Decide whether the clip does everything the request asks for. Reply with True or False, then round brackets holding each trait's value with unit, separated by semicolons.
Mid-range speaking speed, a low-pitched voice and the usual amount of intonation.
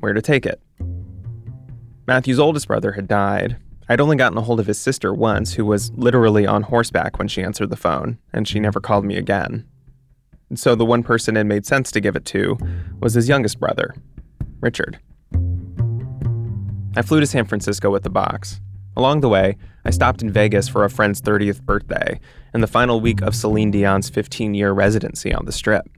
True (195 wpm; 105 Hz; 3.1 semitones)